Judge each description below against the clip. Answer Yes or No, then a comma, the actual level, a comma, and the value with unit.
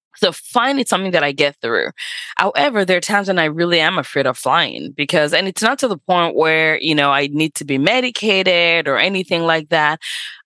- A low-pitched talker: No, medium, 170 Hz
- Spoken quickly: Yes, fast, 220 wpm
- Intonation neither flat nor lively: Yes, average, 3.8 semitones